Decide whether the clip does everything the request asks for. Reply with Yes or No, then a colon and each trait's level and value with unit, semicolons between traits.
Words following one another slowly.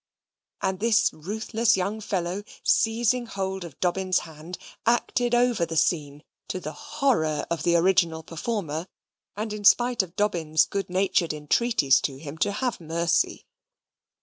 No: average, 145 wpm